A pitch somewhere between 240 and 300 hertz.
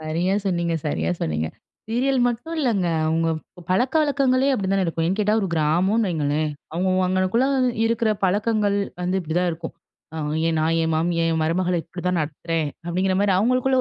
No: medium, 185 Hz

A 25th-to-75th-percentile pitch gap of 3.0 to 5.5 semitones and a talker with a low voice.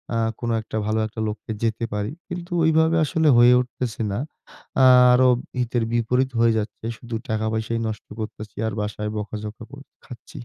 No: narrow, 2.6 semitones; low, 115 Hz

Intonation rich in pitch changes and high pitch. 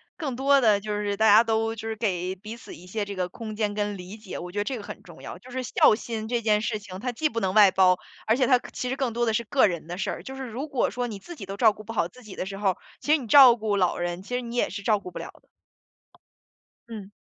No: average, 3.4 semitones; high, 215 Hz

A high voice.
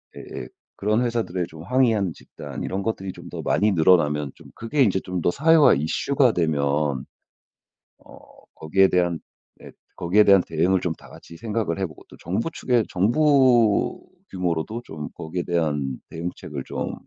No: very low, 90 Hz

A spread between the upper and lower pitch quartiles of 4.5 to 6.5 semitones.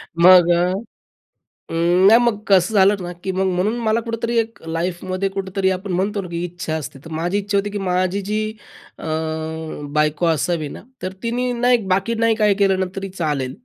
No: average, 3.0 semitones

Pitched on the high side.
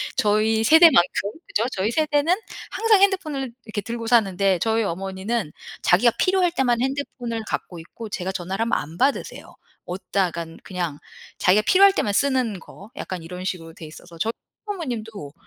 Yes: high, 220 Hz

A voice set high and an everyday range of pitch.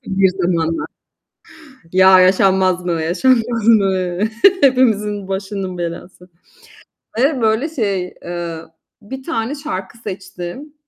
Yes: high, 195 Hz; average, 4.0 semitones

